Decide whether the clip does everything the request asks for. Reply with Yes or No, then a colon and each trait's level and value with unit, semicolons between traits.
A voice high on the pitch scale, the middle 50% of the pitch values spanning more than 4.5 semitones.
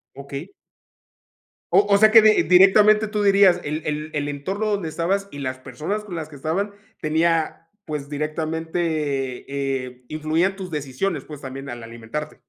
No: medium, 155 Hz; wide, 5.4 semitones